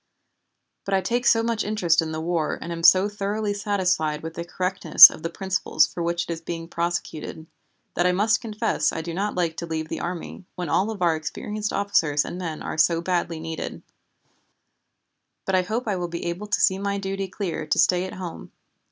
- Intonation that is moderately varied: Yes, average, 3.3 semitones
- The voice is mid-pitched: Yes, medium, 180 Hz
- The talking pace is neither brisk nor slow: No, fast, 210 wpm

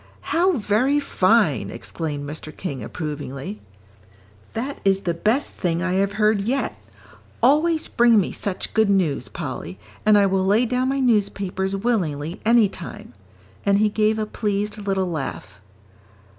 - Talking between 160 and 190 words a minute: No, average, 145 wpm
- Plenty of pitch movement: No, average, 4.3 semitones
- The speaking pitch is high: Yes, high, 200 Hz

